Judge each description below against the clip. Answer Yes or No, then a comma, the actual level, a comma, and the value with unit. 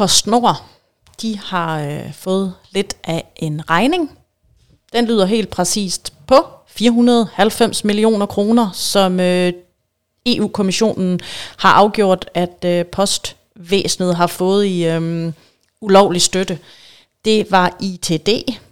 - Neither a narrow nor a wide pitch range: Yes, average, 3.2 semitones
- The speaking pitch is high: Yes, high, 195 Hz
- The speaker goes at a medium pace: No, slow, 105 wpm